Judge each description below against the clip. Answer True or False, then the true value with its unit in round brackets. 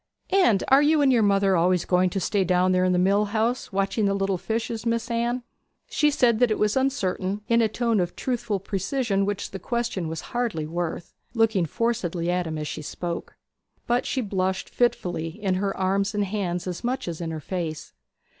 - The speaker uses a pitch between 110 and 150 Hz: False (195 Hz)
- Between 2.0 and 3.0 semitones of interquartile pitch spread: False (4.3 semitones)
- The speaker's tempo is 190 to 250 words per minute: True (200 wpm)